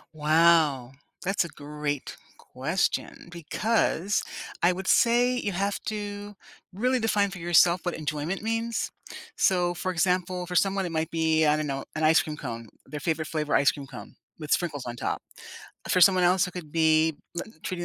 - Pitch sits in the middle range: Yes, medium, 170 Hz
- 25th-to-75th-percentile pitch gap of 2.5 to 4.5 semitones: Yes, average, 3.9 semitones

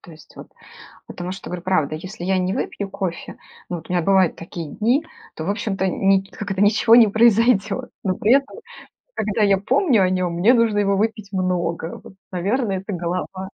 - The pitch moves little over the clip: No, average, 3.0 semitones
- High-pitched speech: Yes, high, 195 Hz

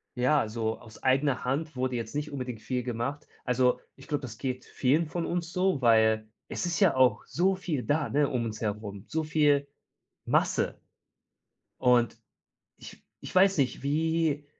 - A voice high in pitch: No, low, 135 Hz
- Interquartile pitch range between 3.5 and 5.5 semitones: Yes, average, 4.3 semitones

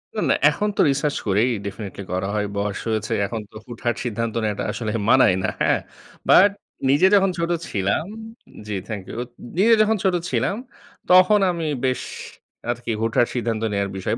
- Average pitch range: No, wide, 7.3 semitones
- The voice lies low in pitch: Yes, low, 115 Hz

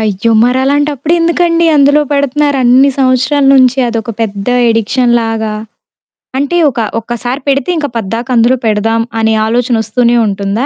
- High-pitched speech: Yes, high, 245 Hz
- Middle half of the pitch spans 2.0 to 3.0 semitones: No, average, 3.8 semitones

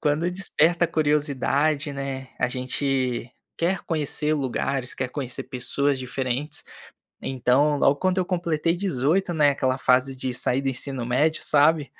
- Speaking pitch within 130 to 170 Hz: Yes, medium, 140 Hz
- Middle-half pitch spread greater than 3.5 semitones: No, average, 3.2 semitones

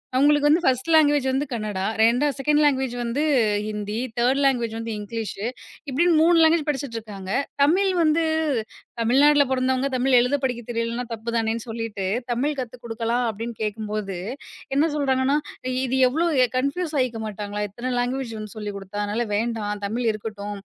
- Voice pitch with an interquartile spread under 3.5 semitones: No, average, 4.2 semitones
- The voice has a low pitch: No, high, 240 Hz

